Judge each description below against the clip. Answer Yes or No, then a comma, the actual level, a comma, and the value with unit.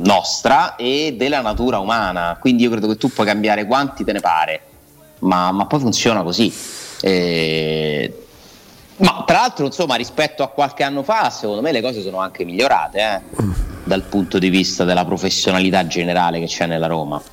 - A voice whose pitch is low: Yes, very low, 95 Hz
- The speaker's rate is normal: No, fast, 175 wpm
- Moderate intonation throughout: No, wide, 5.8 semitones